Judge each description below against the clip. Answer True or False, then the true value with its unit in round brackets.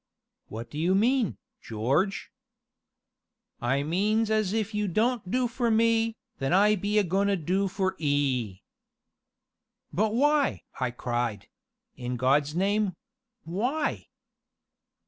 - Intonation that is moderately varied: False (7.4 semitones)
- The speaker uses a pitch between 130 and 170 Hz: False (195 Hz)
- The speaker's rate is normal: False (125 wpm)